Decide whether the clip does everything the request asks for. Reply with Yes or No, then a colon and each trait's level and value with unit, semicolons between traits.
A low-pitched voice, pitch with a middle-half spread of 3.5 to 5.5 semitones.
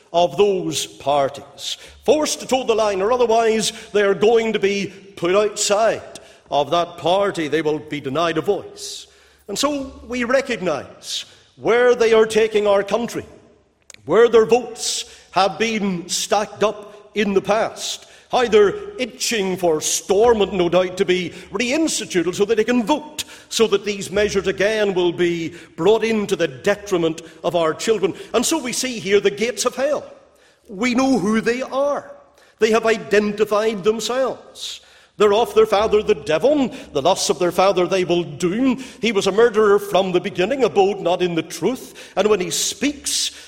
No: high, 205 Hz; average, 4.0 semitones